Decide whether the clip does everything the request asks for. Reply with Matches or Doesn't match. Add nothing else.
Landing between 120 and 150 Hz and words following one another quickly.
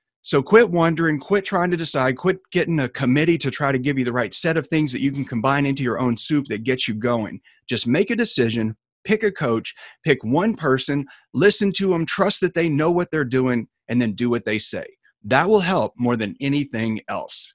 Matches